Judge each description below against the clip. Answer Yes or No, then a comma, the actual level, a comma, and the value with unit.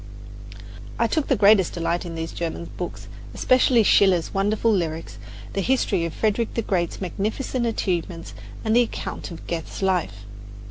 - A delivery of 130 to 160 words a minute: Yes, average, 150 wpm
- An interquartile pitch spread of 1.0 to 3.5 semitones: No, average, 4.6 semitones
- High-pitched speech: Yes, high, 195 Hz